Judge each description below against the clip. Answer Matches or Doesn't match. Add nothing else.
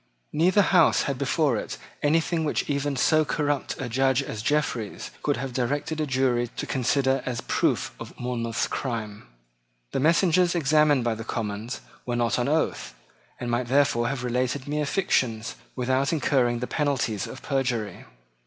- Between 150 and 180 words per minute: Matches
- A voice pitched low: Matches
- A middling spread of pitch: Matches